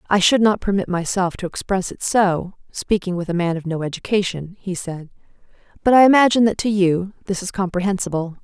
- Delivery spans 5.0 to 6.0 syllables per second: Yes, 5.7 syllables/s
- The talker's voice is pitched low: No, high, 190 Hz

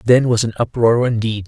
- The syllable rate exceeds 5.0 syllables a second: Yes, 5.2 syllables/s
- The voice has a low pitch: Yes, low, 115 Hz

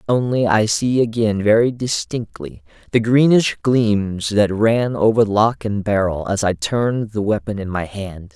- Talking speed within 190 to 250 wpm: No, average, 165 wpm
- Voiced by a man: Yes, male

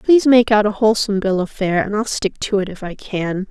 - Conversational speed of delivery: No, fast, 275 wpm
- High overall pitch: Yes, high, 205 Hz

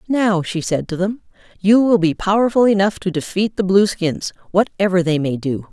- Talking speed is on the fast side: No, average, 190 wpm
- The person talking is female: Yes, female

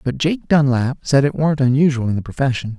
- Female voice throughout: No, male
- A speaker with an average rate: No, fast, 215 wpm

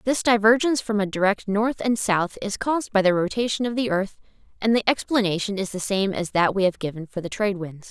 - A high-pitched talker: Yes, high, 205 Hz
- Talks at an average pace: No, fast, 235 wpm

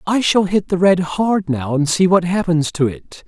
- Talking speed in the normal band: No, fast, 240 wpm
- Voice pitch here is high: No, medium, 175 Hz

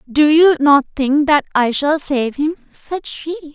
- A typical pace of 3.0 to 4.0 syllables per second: Yes, 3.9 syllables/s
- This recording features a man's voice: No, female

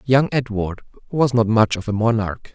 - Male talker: Yes, male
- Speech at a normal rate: Yes, average, 190 wpm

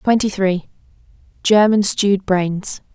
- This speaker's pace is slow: Yes, slow, 80 wpm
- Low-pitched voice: No, high, 195 Hz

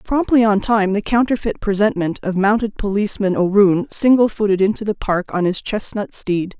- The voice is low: No, high, 205 Hz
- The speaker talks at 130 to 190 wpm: Yes, average, 175 wpm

